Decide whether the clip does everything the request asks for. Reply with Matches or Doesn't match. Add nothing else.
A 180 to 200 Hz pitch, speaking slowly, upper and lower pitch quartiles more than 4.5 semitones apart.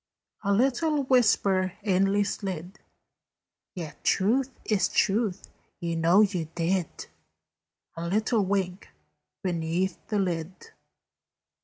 Doesn't match